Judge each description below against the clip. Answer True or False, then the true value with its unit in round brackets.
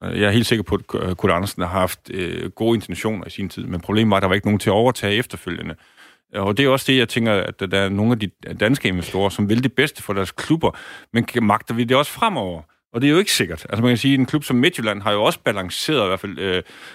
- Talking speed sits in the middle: False (280 wpm)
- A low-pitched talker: True (105 Hz)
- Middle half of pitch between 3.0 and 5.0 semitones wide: True (3.6 semitones)